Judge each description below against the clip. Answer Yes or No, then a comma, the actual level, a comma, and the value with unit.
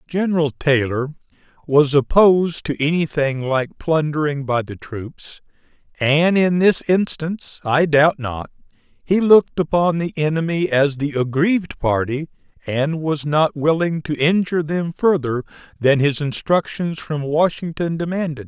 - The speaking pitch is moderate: Yes, medium, 155 Hz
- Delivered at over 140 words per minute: No, slow, 135 wpm